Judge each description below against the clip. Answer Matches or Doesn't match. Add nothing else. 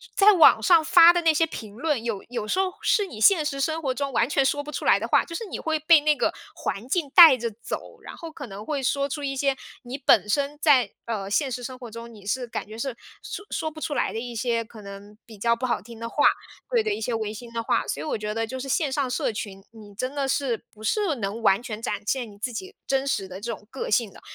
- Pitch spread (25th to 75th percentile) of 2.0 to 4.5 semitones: Doesn't match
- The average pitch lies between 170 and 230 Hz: Doesn't match